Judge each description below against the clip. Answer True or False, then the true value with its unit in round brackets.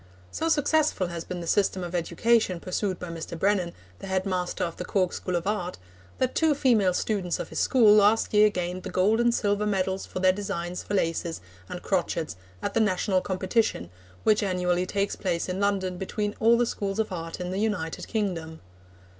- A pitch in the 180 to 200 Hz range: True (190 Hz)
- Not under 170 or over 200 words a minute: True (195 wpm)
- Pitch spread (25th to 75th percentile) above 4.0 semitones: False (2.9 semitones)